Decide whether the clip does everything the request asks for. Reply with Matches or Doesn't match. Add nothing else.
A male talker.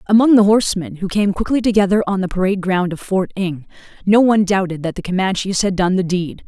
Doesn't match